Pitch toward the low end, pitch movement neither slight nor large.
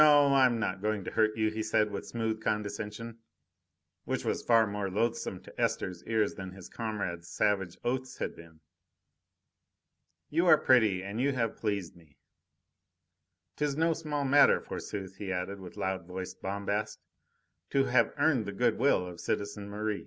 Yes: low, 105 Hz; average, 4.0 semitones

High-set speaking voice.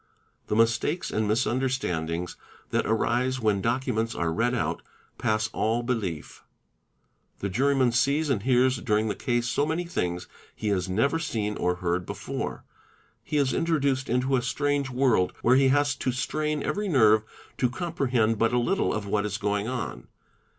No: low, 120 Hz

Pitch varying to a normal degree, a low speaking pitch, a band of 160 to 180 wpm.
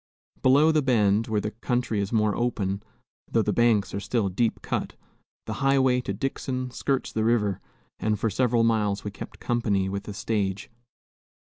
Yes: average, 3.3 semitones; low, 110 Hz; average, 170 wpm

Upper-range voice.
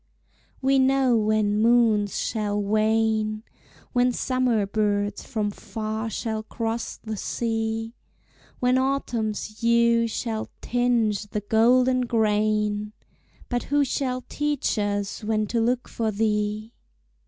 Yes: high, 220 Hz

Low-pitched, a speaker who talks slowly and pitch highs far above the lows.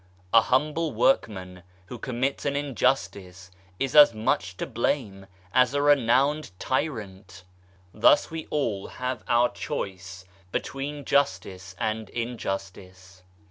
Yes: low, 120 Hz; slow, 115 wpm; wide, 6.3 semitones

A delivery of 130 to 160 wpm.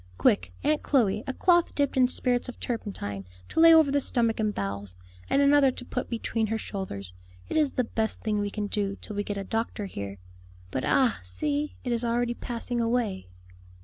No: average, 200 wpm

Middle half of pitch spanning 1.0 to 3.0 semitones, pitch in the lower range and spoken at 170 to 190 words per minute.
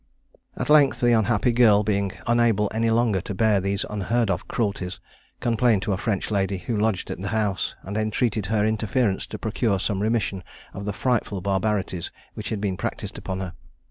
Yes: narrow, 2.6 semitones; low, 105 Hz; average, 185 wpm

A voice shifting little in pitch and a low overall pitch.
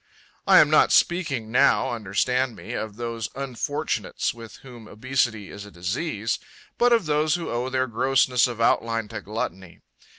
No: average, 3.6 semitones; low, 120 Hz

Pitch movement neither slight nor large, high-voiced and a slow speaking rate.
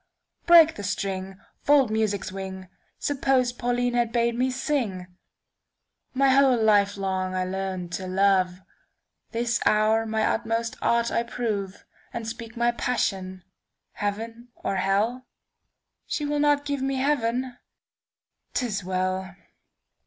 Yes: average, 4.4 semitones; high, 225 Hz; slow, 110 wpm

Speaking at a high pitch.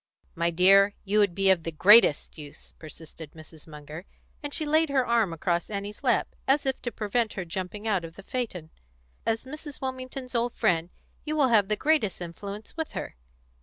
Yes: high, 205 Hz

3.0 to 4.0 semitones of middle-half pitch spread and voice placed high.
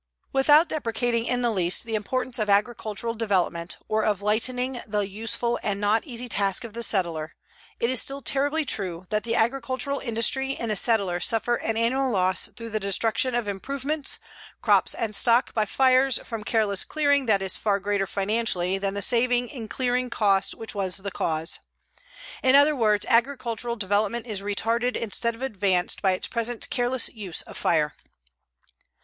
Yes: average, 3.6 semitones; high, 225 Hz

